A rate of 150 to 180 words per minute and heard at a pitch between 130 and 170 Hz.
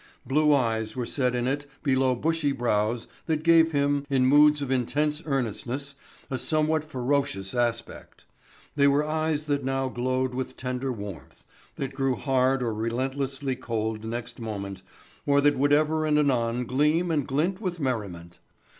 Yes: average, 155 wpm; low, 135 Hz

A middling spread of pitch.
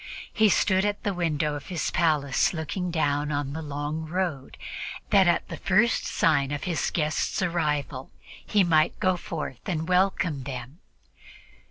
Yes: average, 3.8 semitones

